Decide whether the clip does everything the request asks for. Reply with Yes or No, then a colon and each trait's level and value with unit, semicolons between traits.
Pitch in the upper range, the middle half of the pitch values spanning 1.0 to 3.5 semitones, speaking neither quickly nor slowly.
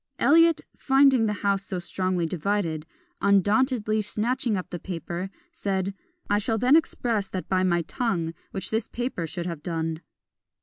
No: high, 200 Hz; average, 4.6 semitones; average, 150 wpm